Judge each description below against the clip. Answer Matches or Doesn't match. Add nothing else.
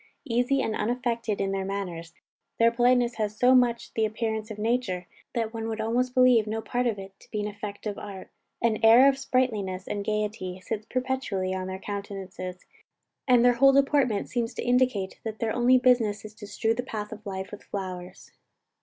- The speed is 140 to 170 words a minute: Doesn't match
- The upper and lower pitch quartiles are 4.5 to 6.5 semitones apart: Doesn't match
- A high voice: Matches